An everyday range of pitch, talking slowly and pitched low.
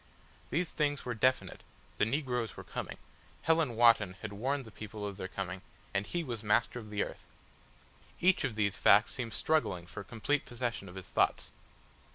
No: average, 4.7 semitones; average, 180 wpm; low, 115 Hz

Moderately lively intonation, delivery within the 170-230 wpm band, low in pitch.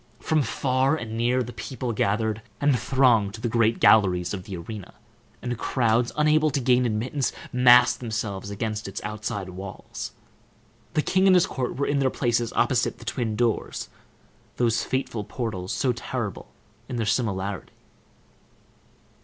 No: average, 3.3 semitones; average, 150 wpm; low, 120 Hz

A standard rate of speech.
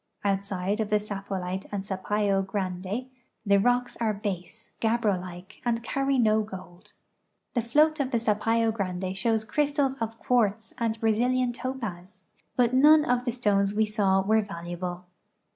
Yes: average, 150 wpm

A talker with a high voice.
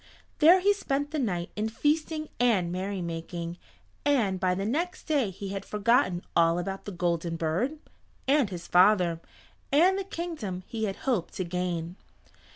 Yes: high, 195 Hz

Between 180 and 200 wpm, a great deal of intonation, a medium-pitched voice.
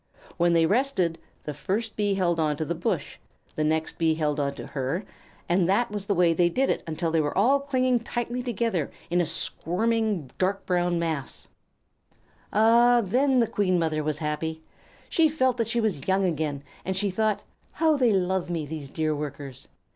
Yes: average, 185 wpm; wide, 6.0 semitones; medium, 180 Hz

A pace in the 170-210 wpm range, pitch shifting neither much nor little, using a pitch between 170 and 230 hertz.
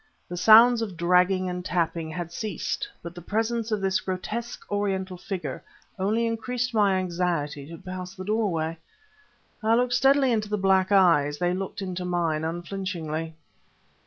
No: average, 155 wpm; average, 3.7 semitones; medium, 185 Hz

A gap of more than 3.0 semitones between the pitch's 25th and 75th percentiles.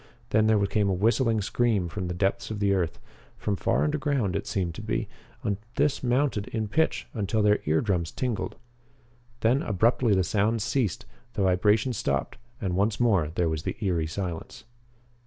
Yes: average, 3.8 semitones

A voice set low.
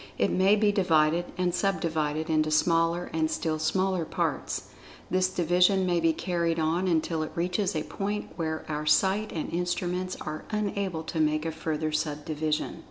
No: medium, 165 Hz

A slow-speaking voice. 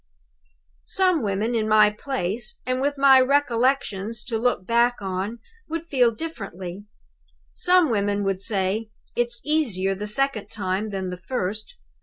No: average, 145 wpm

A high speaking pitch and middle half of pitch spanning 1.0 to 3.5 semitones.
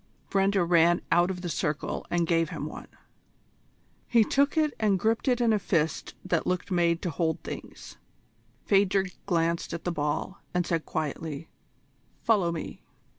No: medium, 175 Hz; average, 3.1 semitones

